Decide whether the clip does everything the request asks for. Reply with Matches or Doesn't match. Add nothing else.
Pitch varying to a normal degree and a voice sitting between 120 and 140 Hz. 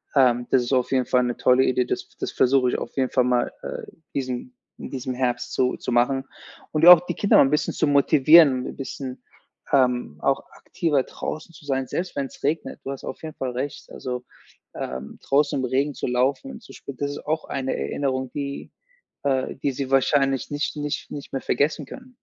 Doesn't match